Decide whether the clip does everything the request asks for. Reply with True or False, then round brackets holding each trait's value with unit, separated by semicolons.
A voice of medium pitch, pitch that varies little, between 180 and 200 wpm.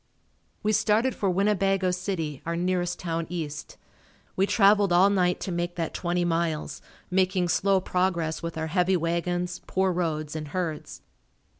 False (180 Hz; 2.2 semitones; 150 wpm)